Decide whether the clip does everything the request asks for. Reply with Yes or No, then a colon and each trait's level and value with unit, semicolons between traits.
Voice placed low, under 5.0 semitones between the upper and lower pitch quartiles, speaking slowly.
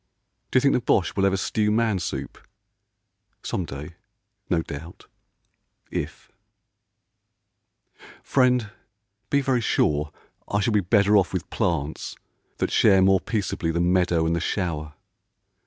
Yes: very low, 95 Hz; average, 4.3 semitones; slow, 130 wpm